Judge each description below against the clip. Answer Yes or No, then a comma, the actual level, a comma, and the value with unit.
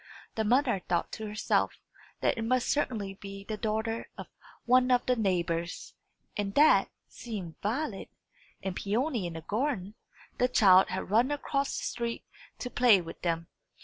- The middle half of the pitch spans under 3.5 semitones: No, average, 4.5 semitones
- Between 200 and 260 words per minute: No, average, 160 wpm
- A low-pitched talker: No, high, 215 Hz